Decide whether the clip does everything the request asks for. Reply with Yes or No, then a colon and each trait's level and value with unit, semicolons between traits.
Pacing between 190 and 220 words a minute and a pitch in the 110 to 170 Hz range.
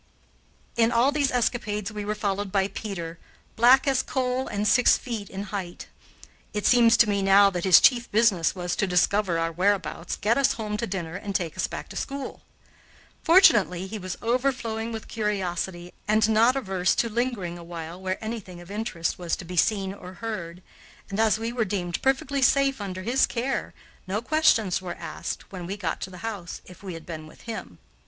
No: average, 195 wpm; high, 205 Hz